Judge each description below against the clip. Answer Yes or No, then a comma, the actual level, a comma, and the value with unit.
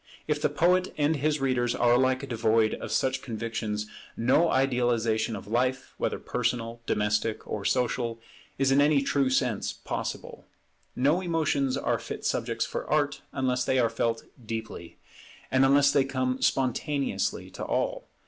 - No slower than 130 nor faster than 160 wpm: Yes, average, 150 wpm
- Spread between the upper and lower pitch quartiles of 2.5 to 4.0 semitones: Yes, average, 3.4 semitones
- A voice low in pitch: Yes, low, 130 Hz